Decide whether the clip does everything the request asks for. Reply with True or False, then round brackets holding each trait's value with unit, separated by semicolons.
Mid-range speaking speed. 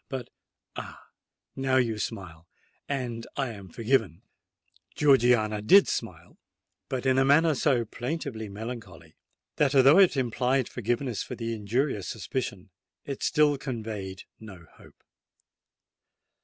False (110 wpm)